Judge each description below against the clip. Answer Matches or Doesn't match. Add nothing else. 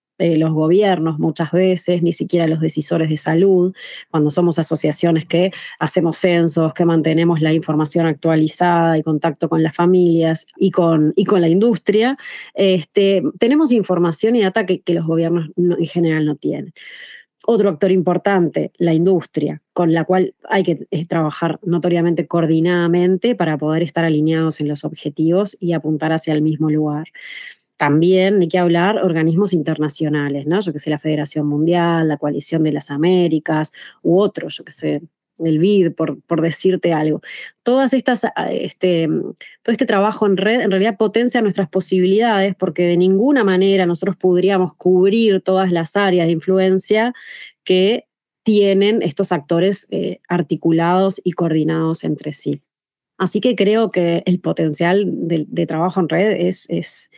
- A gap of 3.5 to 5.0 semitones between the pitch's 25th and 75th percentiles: Doesn't match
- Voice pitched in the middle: Matches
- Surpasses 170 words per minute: Doesn't match